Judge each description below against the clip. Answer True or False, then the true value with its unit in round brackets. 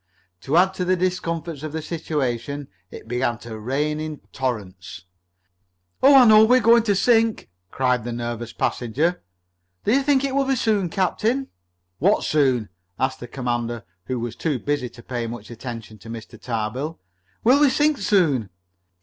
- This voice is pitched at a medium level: True (145 Hz)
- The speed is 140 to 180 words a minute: True (165 wpm)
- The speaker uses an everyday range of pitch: False (8.7 semitones)